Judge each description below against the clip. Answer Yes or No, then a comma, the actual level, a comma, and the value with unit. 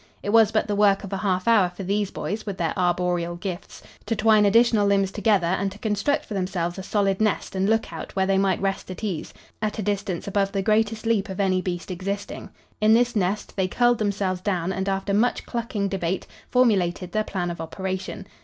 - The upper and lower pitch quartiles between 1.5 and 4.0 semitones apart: Yes, narrow, 2.4 semitones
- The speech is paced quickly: Yes, fast, 210 wpm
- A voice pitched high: Yes, high, 195 Hz